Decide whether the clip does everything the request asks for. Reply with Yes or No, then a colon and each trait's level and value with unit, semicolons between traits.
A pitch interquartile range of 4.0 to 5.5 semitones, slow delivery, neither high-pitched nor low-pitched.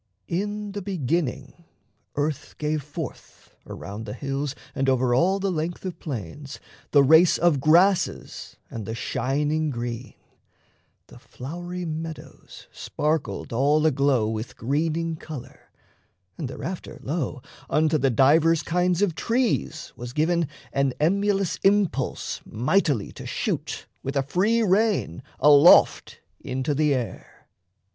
Yes: average, 4.6 semitones; slow, 125 wpm; medium, 155 Hz